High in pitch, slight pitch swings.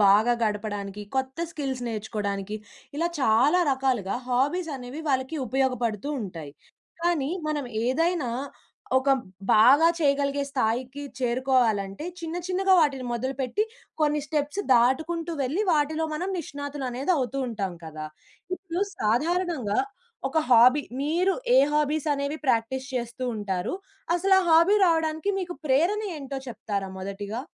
No: very high, 270 Hz; wide, 5.6 semitones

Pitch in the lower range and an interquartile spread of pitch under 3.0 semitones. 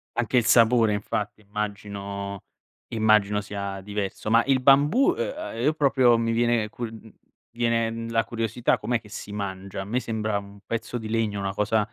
Yes: low, 110 Hz; narrow, 2.4 semitones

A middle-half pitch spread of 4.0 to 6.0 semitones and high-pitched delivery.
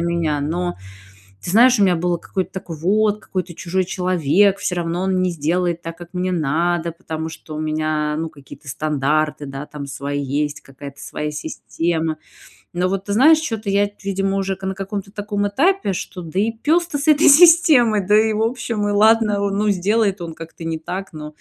No: average, 4.4 semitones; medium, 180 Hz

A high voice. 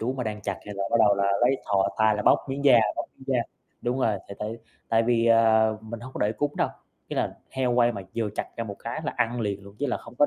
No: low, 115 Hz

